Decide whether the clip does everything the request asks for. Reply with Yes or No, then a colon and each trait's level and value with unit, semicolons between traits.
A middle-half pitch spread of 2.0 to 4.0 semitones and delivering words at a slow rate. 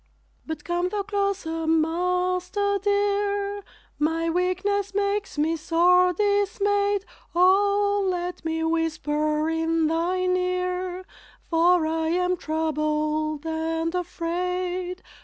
Yes: average, 3.4 semitones; slow, 100 wpm